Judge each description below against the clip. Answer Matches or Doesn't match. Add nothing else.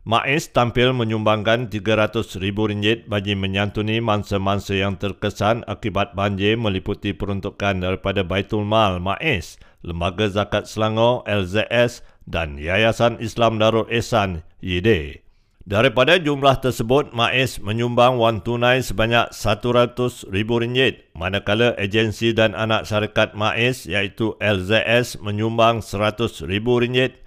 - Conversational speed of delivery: Matches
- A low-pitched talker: Matches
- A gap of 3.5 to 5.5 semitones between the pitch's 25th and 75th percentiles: Doesn't match